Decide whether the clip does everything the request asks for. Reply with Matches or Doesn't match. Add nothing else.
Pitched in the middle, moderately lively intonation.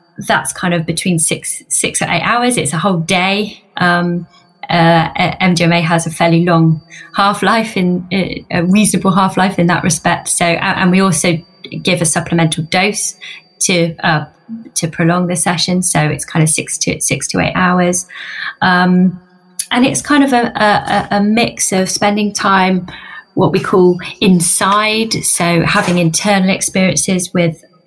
Doesn't match